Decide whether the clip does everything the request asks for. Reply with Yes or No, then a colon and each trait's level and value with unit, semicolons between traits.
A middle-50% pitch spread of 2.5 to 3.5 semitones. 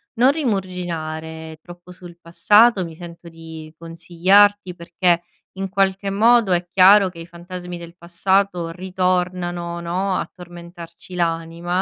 No: narrow, 1.9 semitones